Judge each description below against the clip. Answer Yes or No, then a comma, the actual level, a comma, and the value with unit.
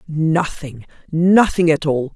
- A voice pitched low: No, medium, 160 Hz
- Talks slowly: Yes, slow, 110 wpm